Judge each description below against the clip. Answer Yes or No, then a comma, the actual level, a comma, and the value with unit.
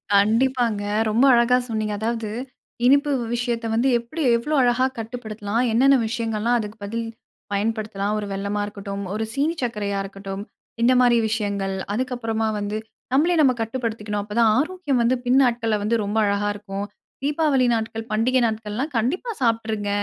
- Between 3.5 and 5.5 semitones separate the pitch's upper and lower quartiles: No, average, 3.1 semitones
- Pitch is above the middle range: Yes, high, 225 Hz